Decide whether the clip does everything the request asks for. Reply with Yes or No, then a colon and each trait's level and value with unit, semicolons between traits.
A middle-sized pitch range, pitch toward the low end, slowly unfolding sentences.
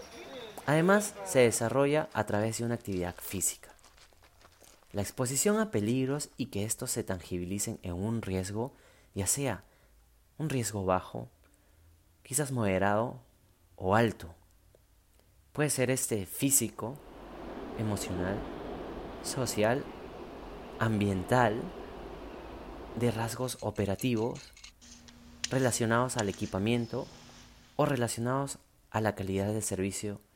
Yes: average, 4.6 semitones; low, 110 Hz; slow, 100 wpm